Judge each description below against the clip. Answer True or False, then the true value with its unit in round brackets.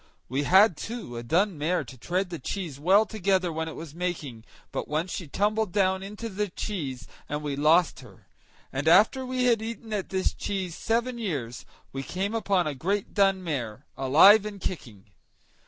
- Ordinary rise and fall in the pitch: False (5.7 semitones)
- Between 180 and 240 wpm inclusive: True (185 wpm)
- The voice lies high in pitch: False (180 Hz)